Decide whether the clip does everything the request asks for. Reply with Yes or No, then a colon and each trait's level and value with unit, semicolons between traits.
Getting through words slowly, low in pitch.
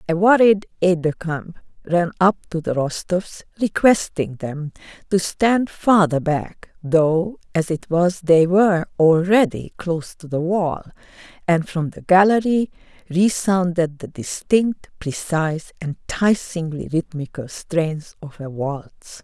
No: slow, 130 wpm; medium, 175 Hz